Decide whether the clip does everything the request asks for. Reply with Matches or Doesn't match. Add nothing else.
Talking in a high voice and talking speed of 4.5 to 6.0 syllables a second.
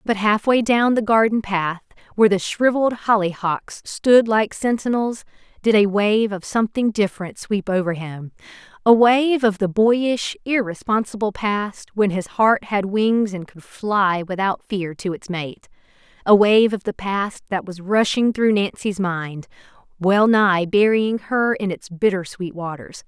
Doesn't match